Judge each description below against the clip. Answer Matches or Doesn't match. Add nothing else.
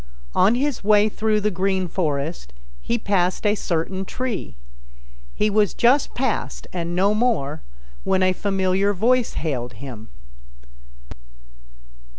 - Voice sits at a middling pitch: Doesn't match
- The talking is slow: Matches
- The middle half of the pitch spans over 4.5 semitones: Doesn't match